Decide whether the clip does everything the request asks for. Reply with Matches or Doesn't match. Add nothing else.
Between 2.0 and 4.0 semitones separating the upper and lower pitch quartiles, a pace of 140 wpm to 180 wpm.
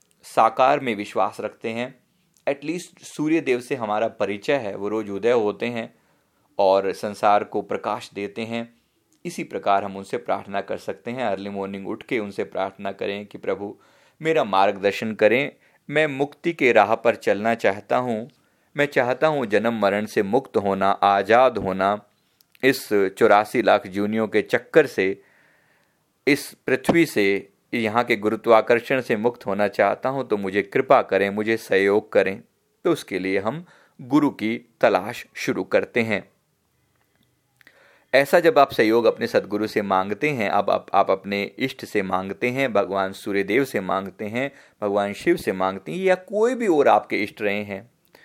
Doesn't match